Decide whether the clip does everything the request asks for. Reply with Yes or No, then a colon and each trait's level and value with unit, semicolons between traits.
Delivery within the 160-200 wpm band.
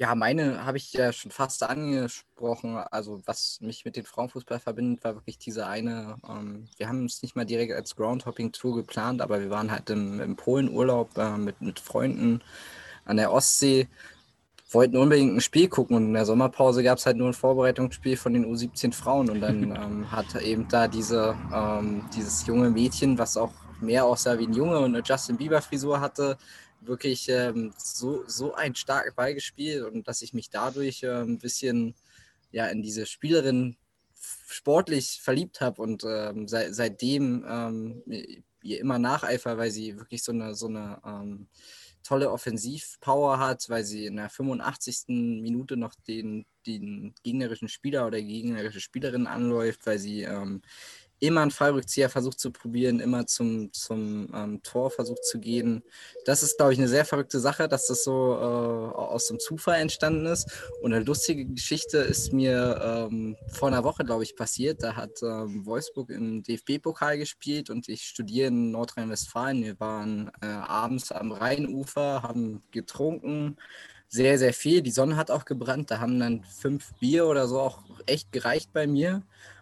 Yes: average, 175 wpm